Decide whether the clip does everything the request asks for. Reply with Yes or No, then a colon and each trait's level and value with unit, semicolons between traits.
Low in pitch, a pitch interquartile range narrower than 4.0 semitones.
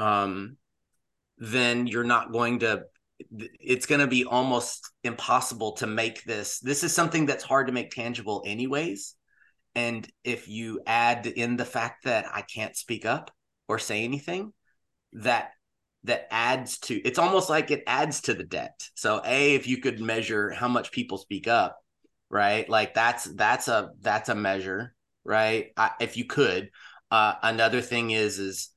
Yes: low, 120 Hz; average, 2.8 semitones